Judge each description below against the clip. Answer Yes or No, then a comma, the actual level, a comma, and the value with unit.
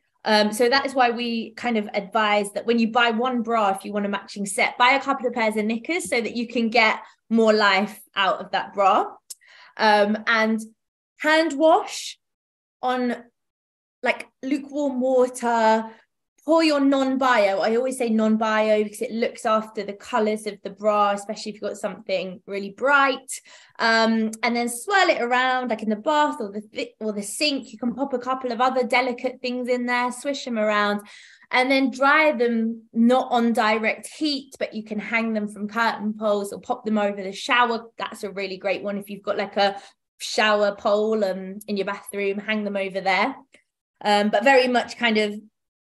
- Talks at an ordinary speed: Yes, average, 195 wpm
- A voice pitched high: Yes, high, 225 Hz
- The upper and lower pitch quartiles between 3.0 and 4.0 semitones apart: Yes, average, 3.3 semitones